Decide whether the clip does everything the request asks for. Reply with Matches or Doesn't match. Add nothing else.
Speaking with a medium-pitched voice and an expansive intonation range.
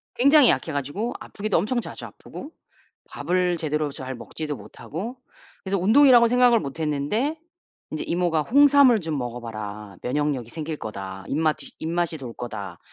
Matches